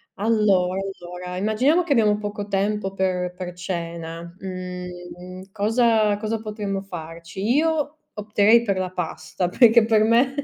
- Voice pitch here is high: Yes, high, 195 Hz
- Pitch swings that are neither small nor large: Yes, average, 3.4 semitones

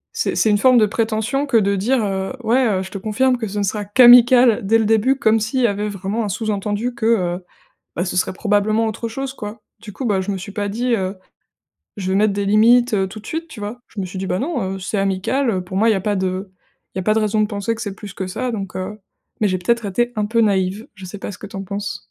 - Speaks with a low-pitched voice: No, high, 210 Hz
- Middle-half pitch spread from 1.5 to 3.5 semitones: Yes, average, 2.9 semitones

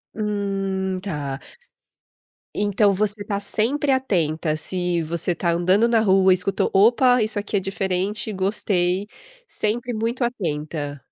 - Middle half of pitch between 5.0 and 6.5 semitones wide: No, average, 3.1 semitones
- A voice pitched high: Yes, high, 195 Hz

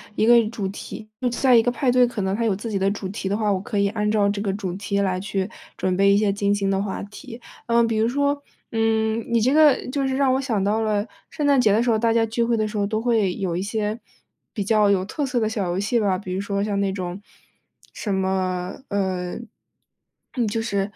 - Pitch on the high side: Yes, high, 210 Hz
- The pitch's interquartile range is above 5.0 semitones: No, average, 2.8 semitones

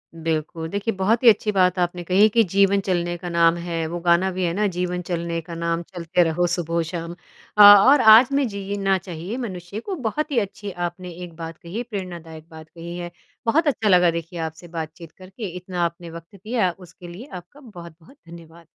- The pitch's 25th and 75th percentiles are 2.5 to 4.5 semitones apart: Yes, average, 3.1 semitones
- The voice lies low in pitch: No, medium, 180 Hz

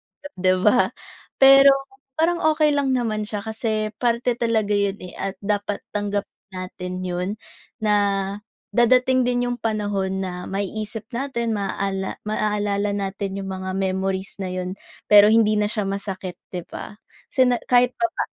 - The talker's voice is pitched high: Yes, high, 210 Hz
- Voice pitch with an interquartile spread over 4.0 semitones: No, average, 3.6 semitones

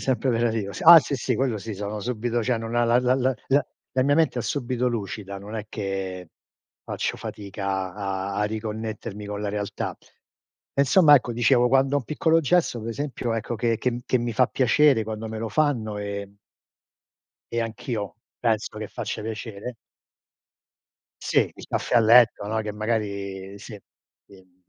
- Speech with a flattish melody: No, average, 3.4 semitones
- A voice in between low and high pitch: No, low, 115 Hz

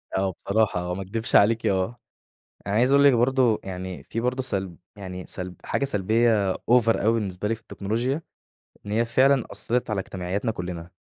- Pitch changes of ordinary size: Yes, average, 4.2 semitones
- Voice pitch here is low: Yes, low, 110 Hz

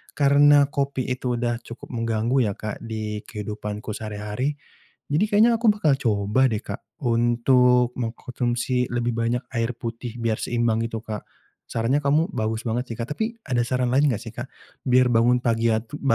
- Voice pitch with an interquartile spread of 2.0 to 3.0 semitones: Yes, narrow, 2.6 semitones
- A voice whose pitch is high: No, low, 120 Hz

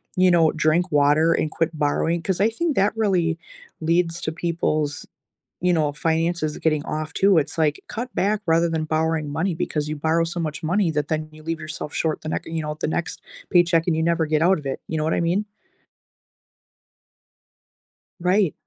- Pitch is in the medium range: Yes, medium, 165 Hz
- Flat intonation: Yes, narrow, 2.0 semitones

